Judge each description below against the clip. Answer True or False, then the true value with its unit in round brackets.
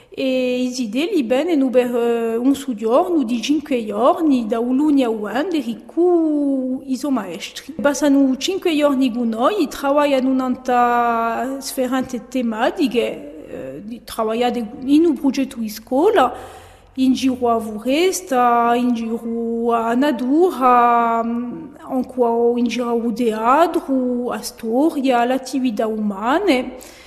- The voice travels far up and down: False (3.0 semitones)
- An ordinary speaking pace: False (115 wpm)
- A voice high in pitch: True (255 Hz)